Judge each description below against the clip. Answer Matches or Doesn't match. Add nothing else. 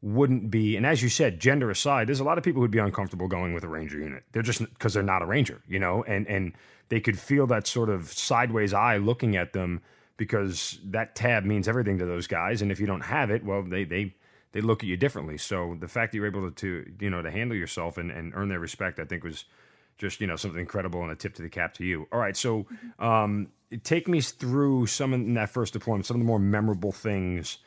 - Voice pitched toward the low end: Matches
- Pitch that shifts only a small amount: Doesn't match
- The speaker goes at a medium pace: Doesn't match